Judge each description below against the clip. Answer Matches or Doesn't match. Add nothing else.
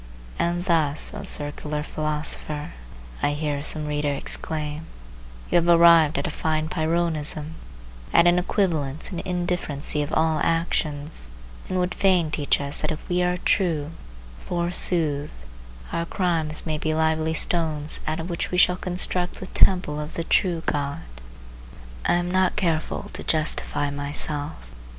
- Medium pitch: Matches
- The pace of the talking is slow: Doesn't match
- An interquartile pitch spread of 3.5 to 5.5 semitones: Doesn't match